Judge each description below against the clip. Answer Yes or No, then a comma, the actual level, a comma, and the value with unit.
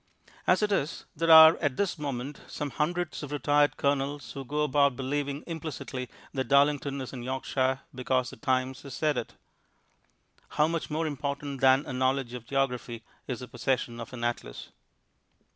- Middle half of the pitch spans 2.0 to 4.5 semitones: Yes, narrow, 2.4 semitones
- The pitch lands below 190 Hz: Yes, medium, 140 Hz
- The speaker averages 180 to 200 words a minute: No, average, 170 wpm